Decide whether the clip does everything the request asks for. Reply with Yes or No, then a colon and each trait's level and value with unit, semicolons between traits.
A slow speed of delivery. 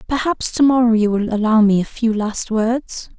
No: fast, 205 wpm